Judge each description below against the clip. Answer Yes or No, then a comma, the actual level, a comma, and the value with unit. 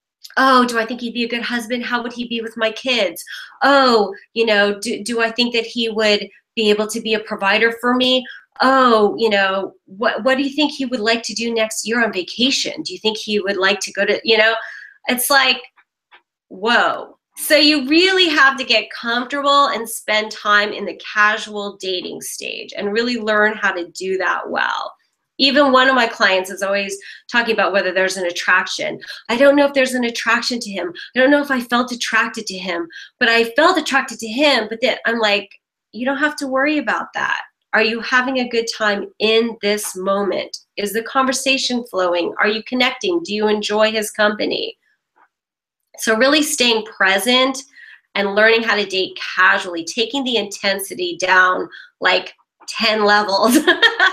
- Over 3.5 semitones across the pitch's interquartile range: Yes, average, 4.1 semitones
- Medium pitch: No, high, 230 Hz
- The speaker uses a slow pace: No, average, 195 wpm